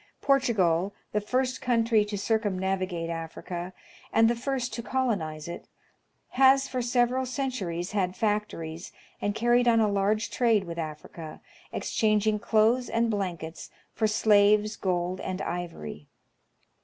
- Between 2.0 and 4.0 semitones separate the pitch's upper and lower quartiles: No, average, 4.9 semitones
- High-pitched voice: Yes, high, 210 Hz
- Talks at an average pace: No, slow, 130 wpm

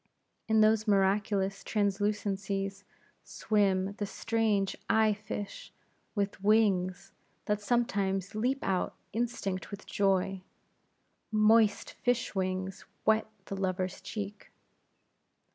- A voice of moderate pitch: No, high, 200 Hz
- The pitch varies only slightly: Yes, narrow, 1.9 semitones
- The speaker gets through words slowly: Yes, slow, 95 wpm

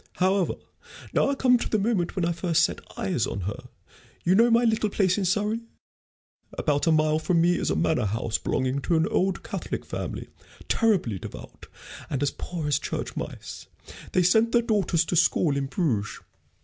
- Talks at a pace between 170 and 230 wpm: Yes, average, 190 wpm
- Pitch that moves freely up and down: Yes, wide, 6.0 semitones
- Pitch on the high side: No, medium, 175 Hz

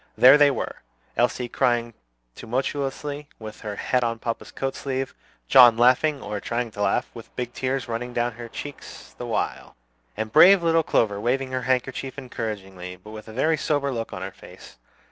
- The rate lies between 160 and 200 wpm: Yes, average, 180 wpm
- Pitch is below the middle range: Yes, low, 125 Hz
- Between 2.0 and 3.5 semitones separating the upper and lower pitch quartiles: Yes, average, 3.0 semitones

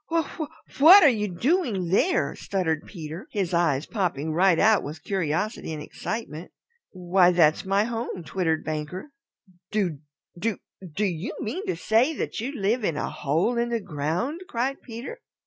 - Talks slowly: No, average, 165 wpm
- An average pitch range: No, wide, 6.2 semitones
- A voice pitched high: Yes, high, 195 Hz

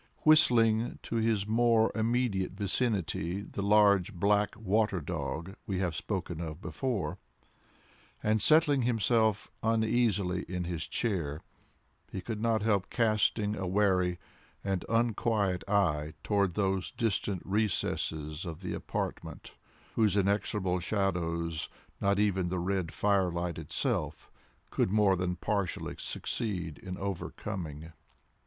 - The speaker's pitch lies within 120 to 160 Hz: No, low, 100 Hz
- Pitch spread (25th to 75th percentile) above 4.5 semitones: No, average, 3.5 semitones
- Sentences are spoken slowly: Yes, slow, 120 wpm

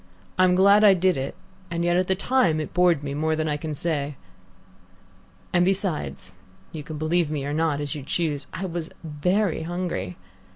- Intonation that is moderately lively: Yes, average, 3.5 semitones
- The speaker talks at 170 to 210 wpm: Yes, average, 190 wpm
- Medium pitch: Yes, medium, 165 Hz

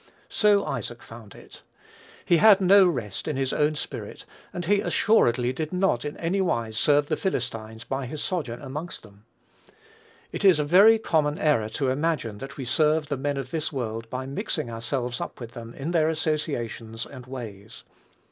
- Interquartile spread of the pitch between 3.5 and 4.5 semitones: No, average, 5.3 semitones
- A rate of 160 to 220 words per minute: Yes, average, 180 wpm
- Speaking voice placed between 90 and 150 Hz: Yes, medium, 140 Hz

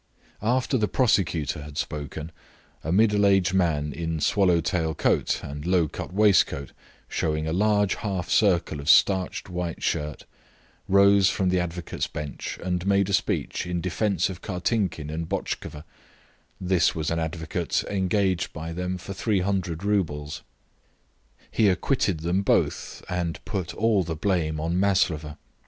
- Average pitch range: Yes, average, 3.5 semitones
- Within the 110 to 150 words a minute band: Yes, average, 145 wpm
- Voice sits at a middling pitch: No, very low, 90 Hz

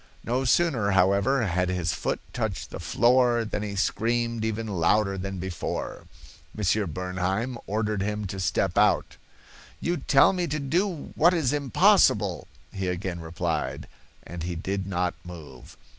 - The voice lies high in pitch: No, low, 100 Hz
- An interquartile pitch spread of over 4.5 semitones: Yes, average, 5.0 semitones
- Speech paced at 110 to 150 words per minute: Yes, average, 145 wpm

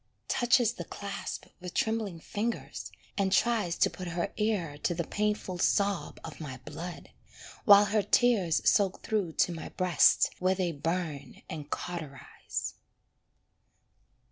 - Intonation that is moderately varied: Yes, average, 3.9 semitones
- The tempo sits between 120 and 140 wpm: Yes, slow, 135 wpm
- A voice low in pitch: No, medium, 185 Hz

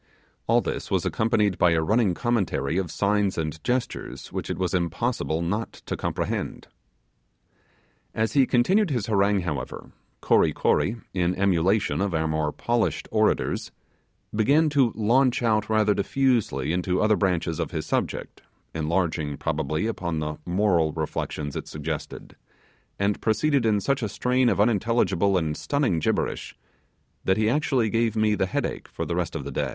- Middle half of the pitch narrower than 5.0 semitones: No, average, 5.3 semitones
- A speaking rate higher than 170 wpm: No, average, 155 wpm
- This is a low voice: Yes, low, 100 Hz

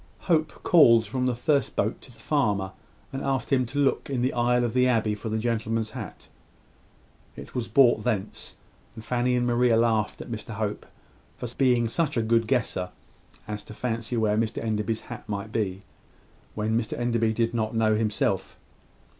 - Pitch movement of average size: No, narrow, 2.3 semitones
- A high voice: No, low, 115 Hz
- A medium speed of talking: Yes, average, 180 wpm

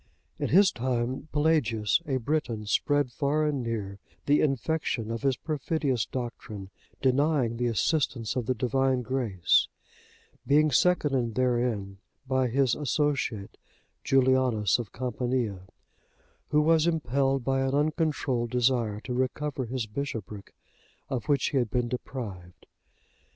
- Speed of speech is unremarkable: No, slow, 125 wpm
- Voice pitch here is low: Yes, low, 130 Hz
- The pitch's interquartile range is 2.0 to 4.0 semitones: Yes, average, 3.5 semitones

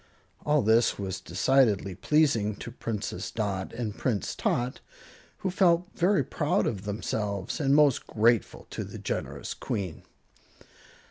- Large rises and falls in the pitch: Yes, wide, 6.0 semitones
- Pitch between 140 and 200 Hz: No, low, 115 Hz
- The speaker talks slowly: Yes, slow, 130 wpm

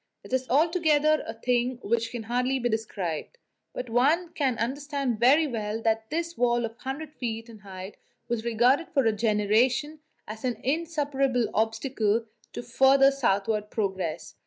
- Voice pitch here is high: Yes, high, 240 Hz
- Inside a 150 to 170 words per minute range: Yes, average, 155 wpm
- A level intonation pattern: No, average, 3.8 semitones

